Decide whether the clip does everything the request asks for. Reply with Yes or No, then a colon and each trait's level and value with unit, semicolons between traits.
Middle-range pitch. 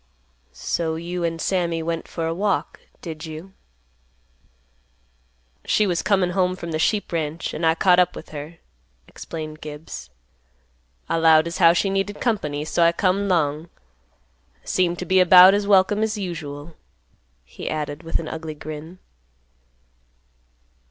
Yes: medium, 170 Hz